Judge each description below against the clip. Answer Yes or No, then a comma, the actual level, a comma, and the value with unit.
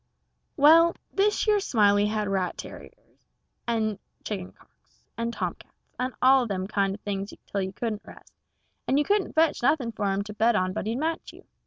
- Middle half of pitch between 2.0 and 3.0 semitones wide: No, wide, 5.5 semitones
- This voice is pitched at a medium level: No, high, 220 Hz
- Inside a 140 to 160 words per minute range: No, average, 190 wpm